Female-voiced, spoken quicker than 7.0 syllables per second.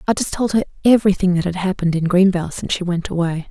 Yes: female; 7.3 syllables/s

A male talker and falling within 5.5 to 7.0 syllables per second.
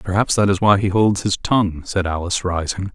Yes: male; 5.8 syllables/s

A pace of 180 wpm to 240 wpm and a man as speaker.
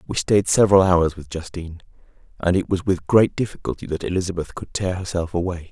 Yes: average, 190 wpm; male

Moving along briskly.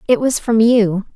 Yes: fast, 210 wpm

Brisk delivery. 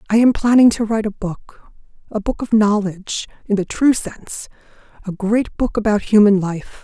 No: average, 165 wpm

